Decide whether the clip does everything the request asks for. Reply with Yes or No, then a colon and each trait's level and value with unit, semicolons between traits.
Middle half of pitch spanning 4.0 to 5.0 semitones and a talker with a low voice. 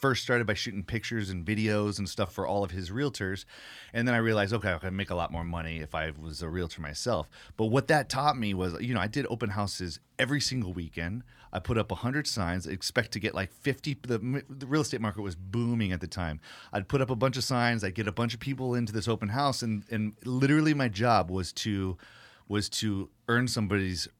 Yes: average, 4.6 semitones; low, 110 Hz